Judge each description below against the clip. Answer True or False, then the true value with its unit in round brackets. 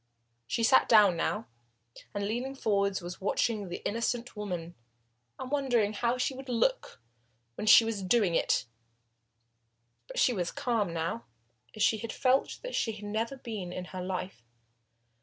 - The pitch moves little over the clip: False (4.0 semitones)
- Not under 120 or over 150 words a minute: False (160 wpm)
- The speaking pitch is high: True (215 Hz)